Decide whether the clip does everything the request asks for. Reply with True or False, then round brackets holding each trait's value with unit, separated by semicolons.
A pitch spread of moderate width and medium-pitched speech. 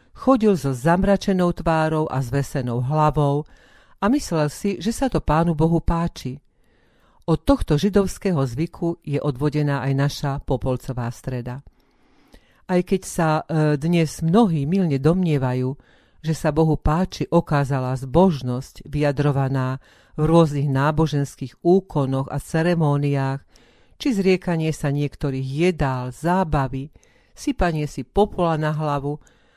True (3.8 semitones; 150 Hz)